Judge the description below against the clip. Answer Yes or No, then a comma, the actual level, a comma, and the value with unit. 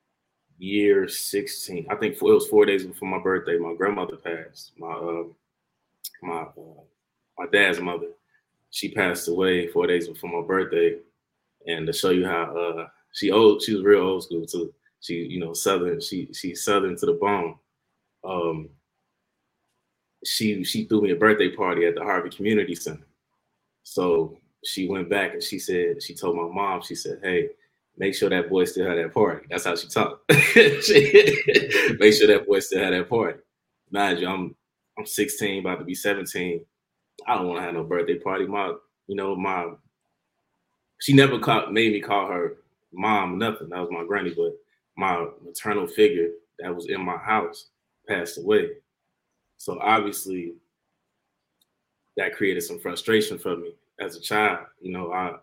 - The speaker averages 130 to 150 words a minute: No, average, 175 wpm